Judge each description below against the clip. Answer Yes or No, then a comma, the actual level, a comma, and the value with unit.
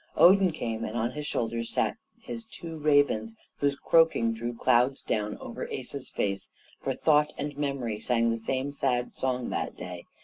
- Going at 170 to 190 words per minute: Yes, average, 175 wpm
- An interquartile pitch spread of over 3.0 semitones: Yes, average, 4.4 semitones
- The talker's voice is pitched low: Yes, low, 125 Hz